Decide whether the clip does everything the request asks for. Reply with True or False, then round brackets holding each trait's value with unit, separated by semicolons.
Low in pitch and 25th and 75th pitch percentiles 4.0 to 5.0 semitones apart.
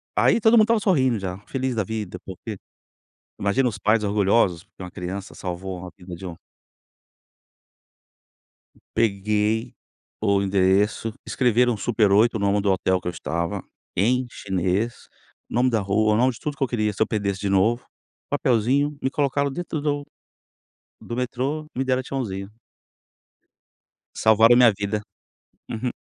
True (110 Hz; 4.4 semitones)